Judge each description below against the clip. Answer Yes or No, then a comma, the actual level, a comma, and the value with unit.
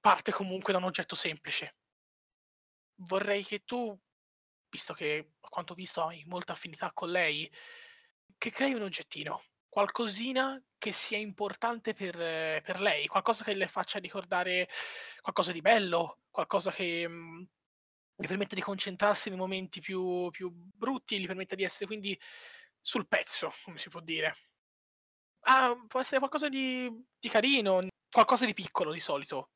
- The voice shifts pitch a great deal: No, average, 4.4 semitones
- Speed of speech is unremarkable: Yes, average, 150 wpm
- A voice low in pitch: No, high, 195 Hz